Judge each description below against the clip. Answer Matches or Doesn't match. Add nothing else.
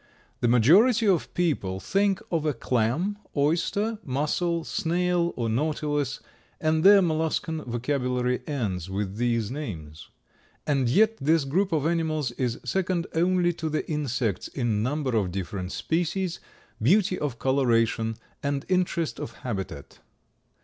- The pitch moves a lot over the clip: Matches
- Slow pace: Matches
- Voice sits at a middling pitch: Matches